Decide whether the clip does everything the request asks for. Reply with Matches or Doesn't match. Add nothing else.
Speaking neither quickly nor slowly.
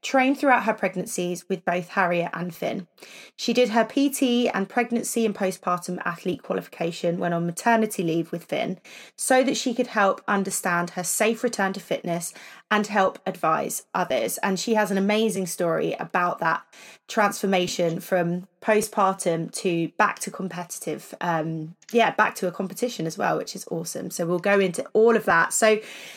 Matches